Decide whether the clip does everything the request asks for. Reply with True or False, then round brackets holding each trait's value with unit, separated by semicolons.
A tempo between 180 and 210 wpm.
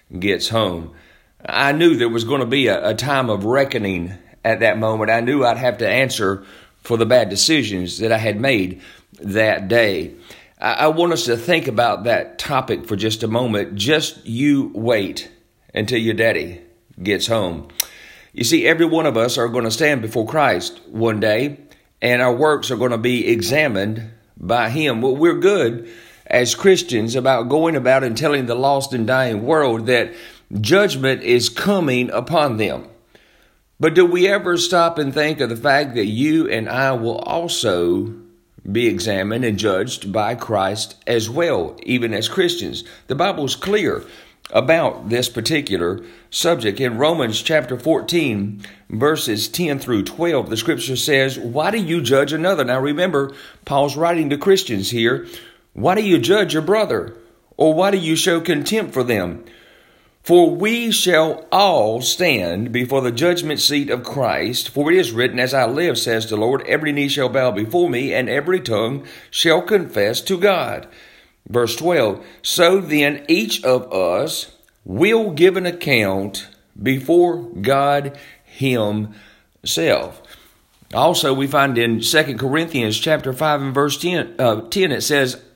False (165 wpm)